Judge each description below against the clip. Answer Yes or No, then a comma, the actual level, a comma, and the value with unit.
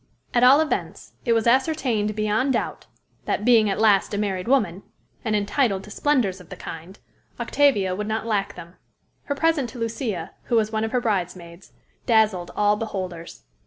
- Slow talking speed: No, average, 175 wpm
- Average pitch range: Yes, average, 3.9 semitones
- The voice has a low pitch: No, high, 215 Hz